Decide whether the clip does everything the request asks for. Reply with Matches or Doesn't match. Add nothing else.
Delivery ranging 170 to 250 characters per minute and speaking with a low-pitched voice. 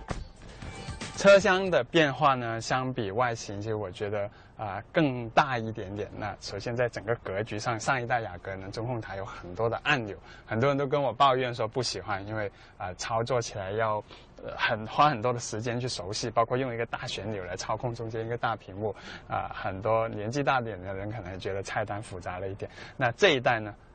Doesn't match